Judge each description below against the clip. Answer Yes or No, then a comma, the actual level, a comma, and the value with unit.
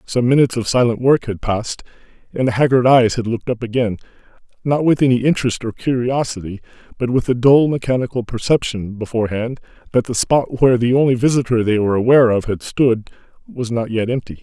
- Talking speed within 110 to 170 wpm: No, average, 185 wpm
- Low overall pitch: Yes, low, 120 Hz